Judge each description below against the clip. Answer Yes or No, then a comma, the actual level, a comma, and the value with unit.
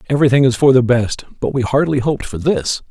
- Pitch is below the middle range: Yes, low, 130 Hz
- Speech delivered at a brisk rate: Yes, fast, 225 wpm